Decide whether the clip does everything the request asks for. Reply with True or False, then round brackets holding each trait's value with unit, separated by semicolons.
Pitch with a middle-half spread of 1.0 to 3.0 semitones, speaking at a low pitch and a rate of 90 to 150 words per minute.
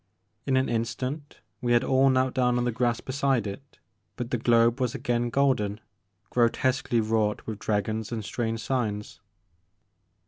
False (2.6 semitones; 120 Hz; 160 wpm)